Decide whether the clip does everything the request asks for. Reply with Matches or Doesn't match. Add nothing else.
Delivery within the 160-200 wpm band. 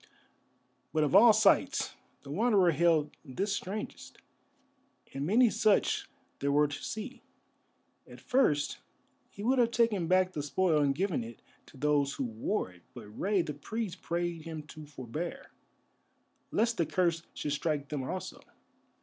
Doesn't match